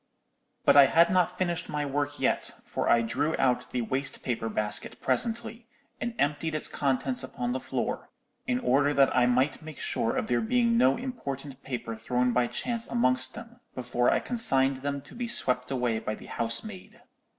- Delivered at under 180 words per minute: No, average, 185 wpm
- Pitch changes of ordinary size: No, wide, 5.9 semitones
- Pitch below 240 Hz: Yes, low, 135 Hz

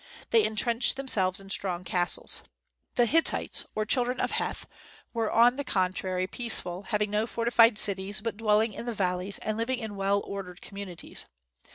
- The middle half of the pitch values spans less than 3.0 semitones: No, average, 3.5 semitones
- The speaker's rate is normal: Yes, average, 165 wpm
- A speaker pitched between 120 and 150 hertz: No, high, 210 Hz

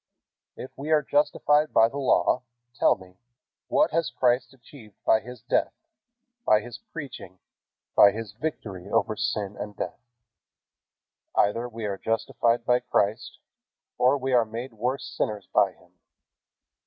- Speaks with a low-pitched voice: Yes, low, 115 Hz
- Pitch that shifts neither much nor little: Yes, average, 4.2 semitones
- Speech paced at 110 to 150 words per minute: Yes, average, 140 wpm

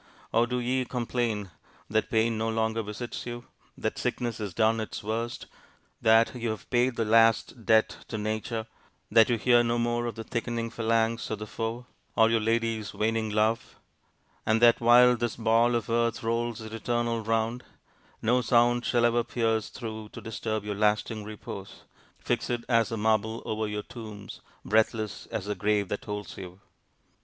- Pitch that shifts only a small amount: Yes, narrow, 1.5 semitones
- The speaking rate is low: No, average, 170 wpm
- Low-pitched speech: Yes, low, 115 Hz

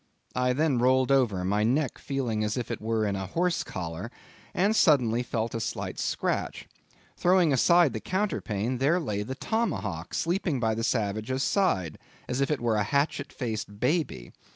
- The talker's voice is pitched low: Yes, low, 125 Hz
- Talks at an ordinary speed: Yes, average, 175 wpm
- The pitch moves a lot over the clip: Yes, wide, 5.7 semitones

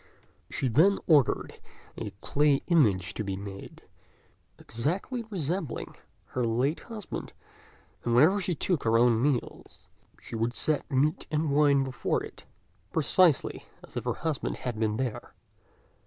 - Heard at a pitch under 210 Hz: Yes, medium, 140 Hz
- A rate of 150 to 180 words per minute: No, average, 140 wpm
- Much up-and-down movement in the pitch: Yes, wide, 5.7 semitones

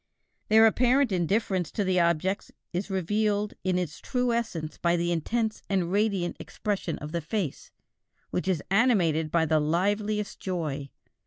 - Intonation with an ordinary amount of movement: Yes, average, 3.9 semitones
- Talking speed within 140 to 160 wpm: Yes, average, 150 wpm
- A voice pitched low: No, medium, 185 Hz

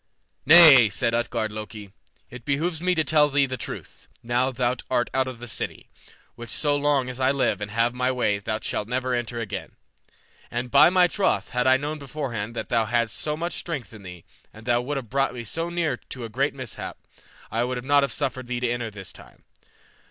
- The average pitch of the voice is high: No, low, 125 Hz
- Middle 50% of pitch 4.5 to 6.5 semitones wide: No, average, 3.4 semitones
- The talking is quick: Yes, fast, 210 wpm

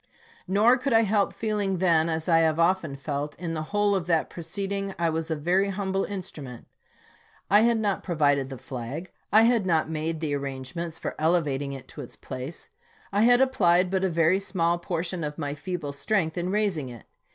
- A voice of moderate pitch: Yes, medium, 170 Hz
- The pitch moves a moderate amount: Yes, average, 4.2 semitones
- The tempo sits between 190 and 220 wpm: Yes, average, 200 wpm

